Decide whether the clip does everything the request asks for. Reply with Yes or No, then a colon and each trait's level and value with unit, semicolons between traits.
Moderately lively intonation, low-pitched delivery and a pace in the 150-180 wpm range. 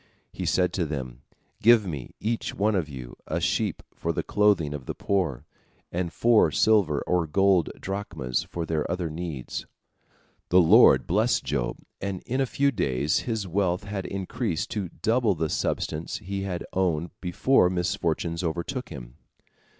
Yes: average, 4.4 semitones; very low, 90 Hz; average, 160 wpm